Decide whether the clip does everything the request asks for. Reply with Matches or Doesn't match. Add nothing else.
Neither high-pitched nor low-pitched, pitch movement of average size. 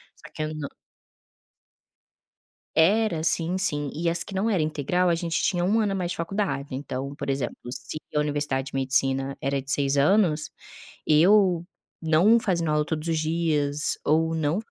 Matches